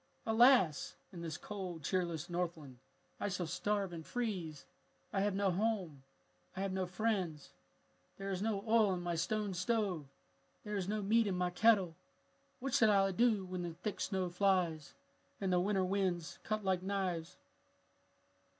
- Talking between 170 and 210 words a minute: No, average, 160 wpm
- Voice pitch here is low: No, high, 190 Hz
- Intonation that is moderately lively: Yes, average, 3.0 semitones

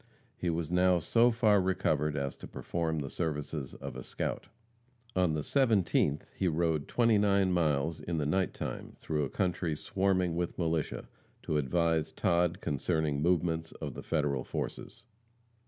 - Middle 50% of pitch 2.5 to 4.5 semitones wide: Yes, average, 3.3 semitones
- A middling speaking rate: Yes, average, 160 wpm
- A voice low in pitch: Yes, very low, 85 Hz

